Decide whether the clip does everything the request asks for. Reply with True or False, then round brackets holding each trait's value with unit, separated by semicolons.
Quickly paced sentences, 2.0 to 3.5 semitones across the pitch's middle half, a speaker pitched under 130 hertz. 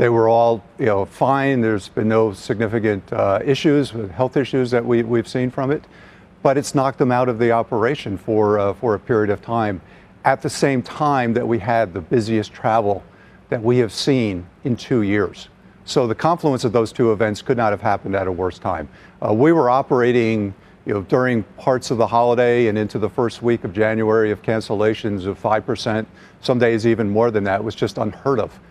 True (210 wpm; 2.8 semitones; 115 Hz)